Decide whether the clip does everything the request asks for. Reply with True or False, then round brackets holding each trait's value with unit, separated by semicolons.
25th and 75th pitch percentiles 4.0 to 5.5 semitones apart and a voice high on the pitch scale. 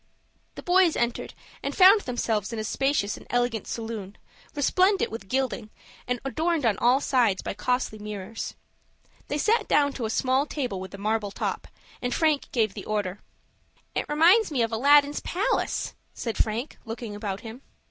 True (5.1 semitones; 245 Hz)